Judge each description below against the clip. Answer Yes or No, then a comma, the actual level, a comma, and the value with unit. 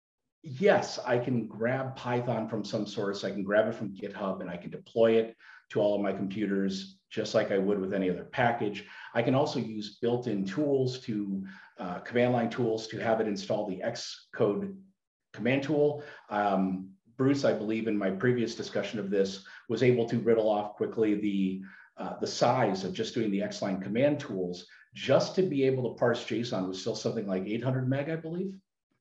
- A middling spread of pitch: Yes, average, 3.9 semitones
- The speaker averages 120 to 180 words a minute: No, average, 190 wpm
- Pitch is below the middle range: Yes, low, 110 Hz